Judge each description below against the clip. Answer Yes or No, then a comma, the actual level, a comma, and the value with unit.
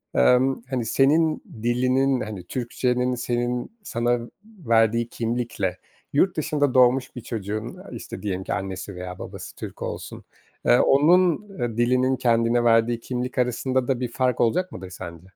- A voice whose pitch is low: Yes, low, 120 Hz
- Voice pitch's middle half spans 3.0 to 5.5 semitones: No, narrow, 2.4 semitones